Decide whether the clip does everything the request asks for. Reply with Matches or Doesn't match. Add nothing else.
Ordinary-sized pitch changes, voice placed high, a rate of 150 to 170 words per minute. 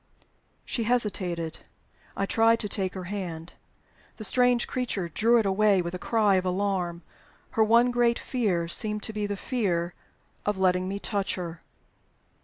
Matches